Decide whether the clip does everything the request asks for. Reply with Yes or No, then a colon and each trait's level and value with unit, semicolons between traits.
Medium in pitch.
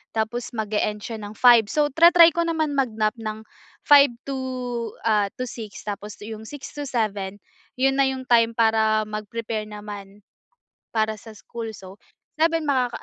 No: high, 225 Hz